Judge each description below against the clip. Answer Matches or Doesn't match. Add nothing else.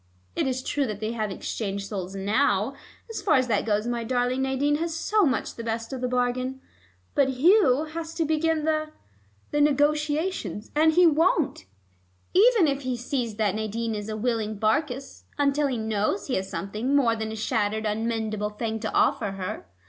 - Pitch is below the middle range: Doesn't match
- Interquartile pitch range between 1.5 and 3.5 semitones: Doesn't match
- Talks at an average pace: Matches